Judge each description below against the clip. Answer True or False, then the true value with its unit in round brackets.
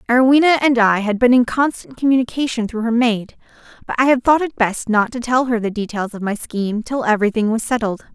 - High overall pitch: True (235 Hz)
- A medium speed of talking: False (220 wpm)